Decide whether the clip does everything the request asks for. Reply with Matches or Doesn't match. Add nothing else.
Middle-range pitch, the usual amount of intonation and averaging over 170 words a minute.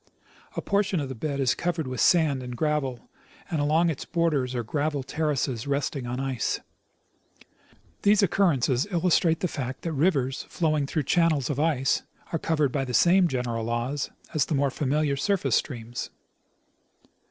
Doesn't match